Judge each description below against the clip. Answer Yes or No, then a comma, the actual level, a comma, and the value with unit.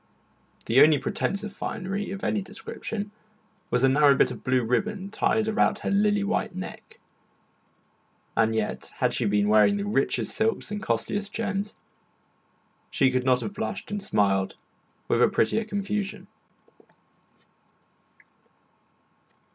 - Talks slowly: Yes, slow, 130 wpm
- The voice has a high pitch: Yes, high, 195 Hz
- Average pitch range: No, wide, 8.5 semitones